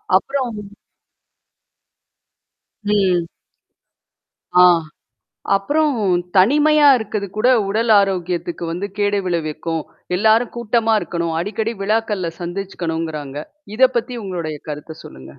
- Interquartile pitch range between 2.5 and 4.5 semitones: No, average, 4.9 semitones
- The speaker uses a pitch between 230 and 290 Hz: No, high, 195 Hz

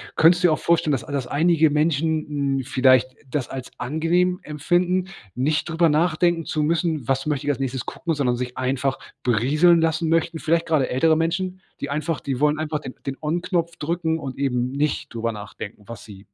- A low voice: No, medium, 150 Hz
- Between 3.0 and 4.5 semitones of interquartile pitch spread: Yes, average, 3.7 semitones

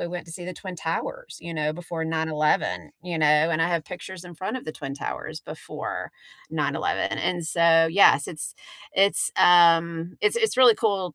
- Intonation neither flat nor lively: No, narrow, 2.2 semitones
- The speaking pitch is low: No, medium, 170 Hz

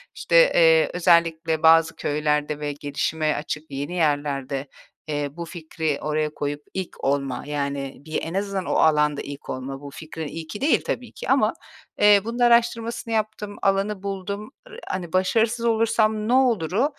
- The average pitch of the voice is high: No, medium, 165 Hz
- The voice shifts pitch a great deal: Yes, wide, 6.3 semitones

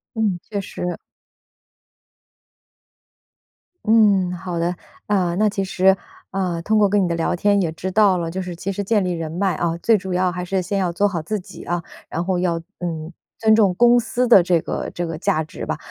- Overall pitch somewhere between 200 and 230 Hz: No, medium, 185 Hz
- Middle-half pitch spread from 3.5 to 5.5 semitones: No, average, 2.8 semitones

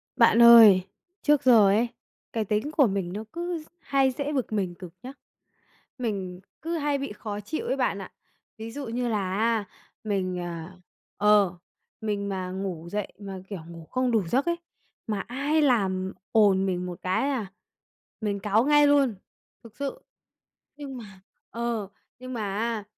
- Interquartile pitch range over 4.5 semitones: Yes, average, 4.9 semitones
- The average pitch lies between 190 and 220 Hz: Yes, high, 215 Hz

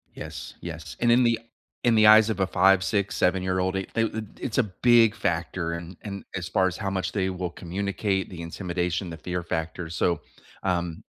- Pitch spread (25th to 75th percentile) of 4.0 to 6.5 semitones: No, average, 3.1 semitones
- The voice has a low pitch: Yes, very low, 95 Hz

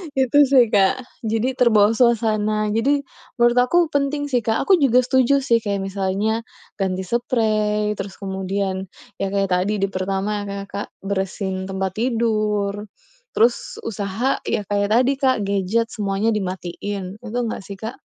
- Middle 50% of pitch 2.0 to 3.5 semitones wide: Yes, average, 3.1 semitones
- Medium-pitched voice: No, high, 210 Hz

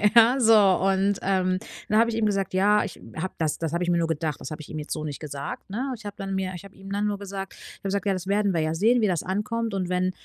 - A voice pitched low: No, high, 195 Hz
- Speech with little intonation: No, average, 3.2 semitones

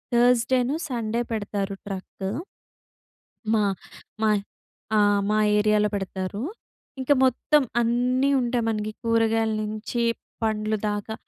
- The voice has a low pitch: No, high, 220 Hz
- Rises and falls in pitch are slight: Yes, narrow, 2.3 semitones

